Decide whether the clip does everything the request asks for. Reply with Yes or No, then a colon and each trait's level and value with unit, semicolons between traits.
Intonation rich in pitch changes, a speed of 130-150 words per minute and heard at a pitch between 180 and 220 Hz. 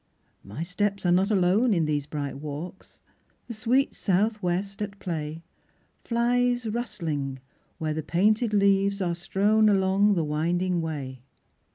No: average, 4.8 semitones; average, 140 wpm; high, 190 Hz